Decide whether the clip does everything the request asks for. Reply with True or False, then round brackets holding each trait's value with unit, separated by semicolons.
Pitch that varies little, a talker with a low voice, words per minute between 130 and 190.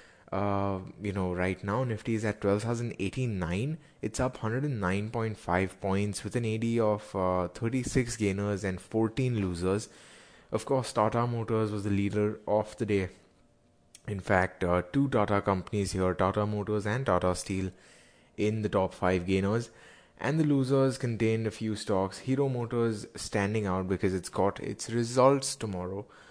False (3.4 semitones; 105 Hz; 155 wpm)